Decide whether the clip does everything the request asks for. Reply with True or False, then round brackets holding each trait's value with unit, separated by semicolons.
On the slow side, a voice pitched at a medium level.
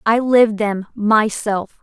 False (130 wpm; 215 Hz)